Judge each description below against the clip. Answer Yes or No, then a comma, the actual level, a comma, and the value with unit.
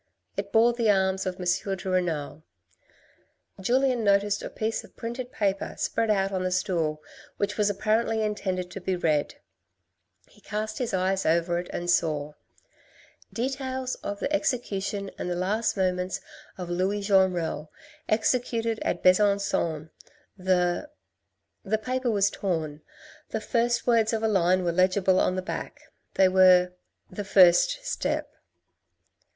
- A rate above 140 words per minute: Yes, average, 155 wpm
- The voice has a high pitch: Yes, high, 195 Hz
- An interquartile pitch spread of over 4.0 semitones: No, average, 3.4 semitones